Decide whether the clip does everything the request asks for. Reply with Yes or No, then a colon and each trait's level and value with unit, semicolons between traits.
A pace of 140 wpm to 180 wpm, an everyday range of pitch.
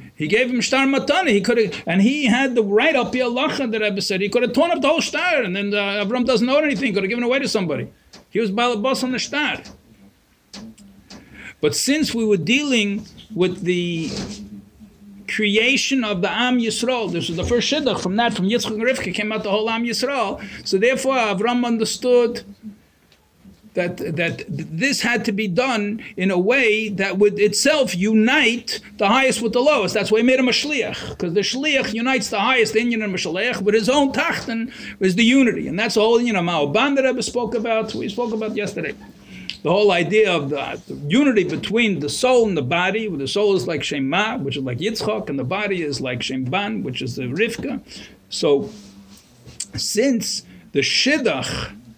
No: average, 200 wpm; average, 4.1 semitones